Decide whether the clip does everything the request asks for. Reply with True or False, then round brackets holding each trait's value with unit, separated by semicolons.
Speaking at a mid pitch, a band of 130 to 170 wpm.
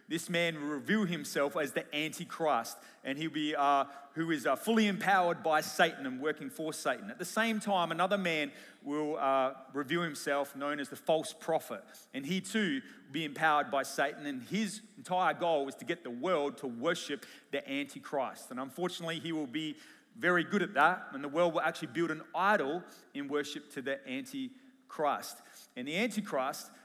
False (165 Hz; 190 wpm)